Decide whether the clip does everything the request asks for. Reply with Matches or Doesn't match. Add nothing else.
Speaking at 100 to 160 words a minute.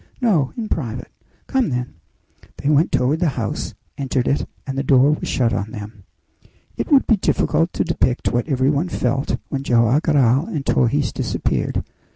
Doesn't match